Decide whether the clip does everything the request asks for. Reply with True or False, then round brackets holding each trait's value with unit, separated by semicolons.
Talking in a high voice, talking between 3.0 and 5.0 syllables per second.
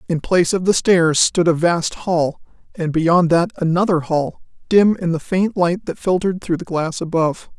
False (170 Hz; 4.8 syllables/s)